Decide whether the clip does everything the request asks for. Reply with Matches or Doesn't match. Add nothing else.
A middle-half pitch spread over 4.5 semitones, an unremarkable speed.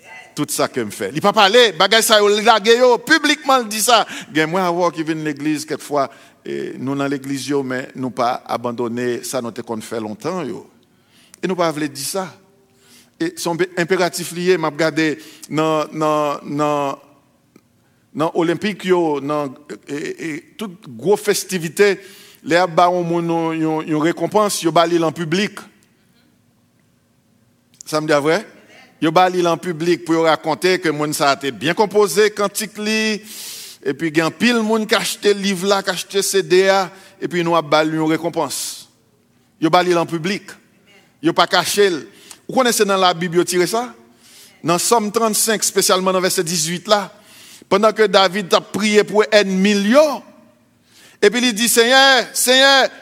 Matches